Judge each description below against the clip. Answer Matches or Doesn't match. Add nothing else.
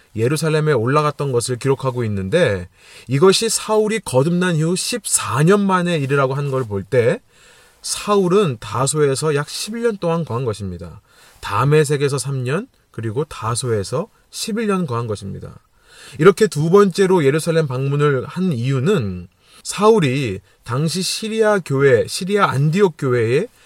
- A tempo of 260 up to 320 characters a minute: Matches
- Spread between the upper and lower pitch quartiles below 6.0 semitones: Doesn't match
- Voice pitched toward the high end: Doesn't match